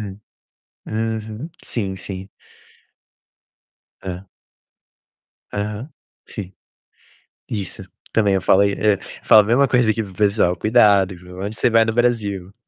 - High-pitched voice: No, low, 105 Hz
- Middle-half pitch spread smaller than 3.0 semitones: Yes, narrow, 2.6 semitones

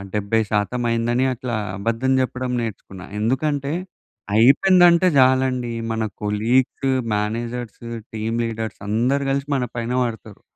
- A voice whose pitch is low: Yes, low, 120 Hz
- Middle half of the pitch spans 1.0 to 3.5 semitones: Yes, average, 2.9 semitones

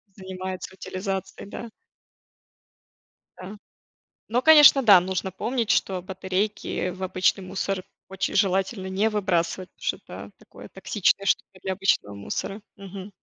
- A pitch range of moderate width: No, narrow, 1.6 semitones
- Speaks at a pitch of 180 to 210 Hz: Yes, high, 190 Hz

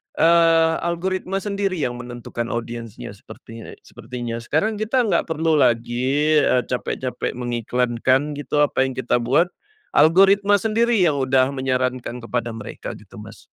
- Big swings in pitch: Yes, wide, 6.0 semitones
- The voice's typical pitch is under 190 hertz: Yes, low, 135 Hz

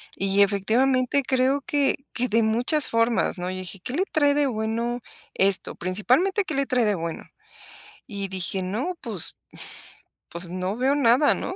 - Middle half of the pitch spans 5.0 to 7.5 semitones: Yes, wide, 5.6 semitones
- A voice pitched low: No, high, 230 Hz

